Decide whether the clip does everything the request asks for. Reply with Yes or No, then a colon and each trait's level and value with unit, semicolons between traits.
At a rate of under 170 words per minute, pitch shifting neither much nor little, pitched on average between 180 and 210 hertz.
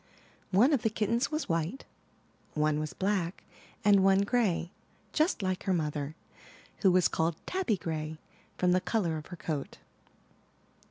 Yes: average, 150 wpm; average, 4.8 semitones; medium, 185 Hz